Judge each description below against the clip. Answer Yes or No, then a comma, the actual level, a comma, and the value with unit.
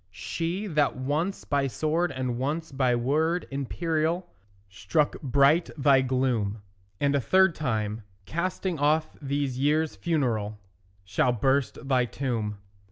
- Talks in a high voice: No, medium, 140 Hz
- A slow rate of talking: Yes, slow, 125 wpm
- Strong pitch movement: No, average, 4.1 semitones